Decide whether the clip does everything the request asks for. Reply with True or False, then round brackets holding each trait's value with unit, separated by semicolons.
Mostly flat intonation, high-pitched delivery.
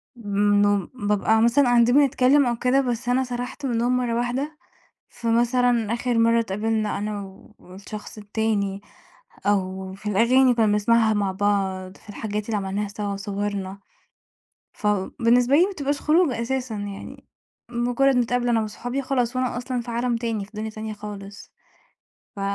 False (3.3 semitones; 230 Hz)